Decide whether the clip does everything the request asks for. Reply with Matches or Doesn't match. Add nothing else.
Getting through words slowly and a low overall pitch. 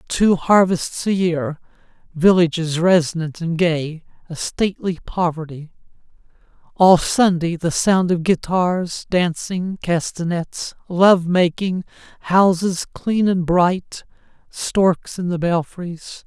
Doesn't match